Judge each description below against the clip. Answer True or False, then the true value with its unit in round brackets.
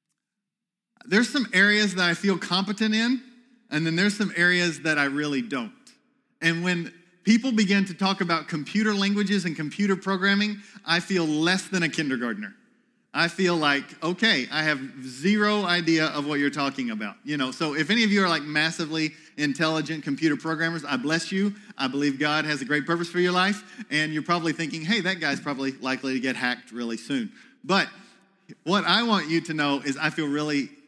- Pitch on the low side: False (170 Hz)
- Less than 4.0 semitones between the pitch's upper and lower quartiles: False (5.4 semitones)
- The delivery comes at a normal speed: True (190 wpm)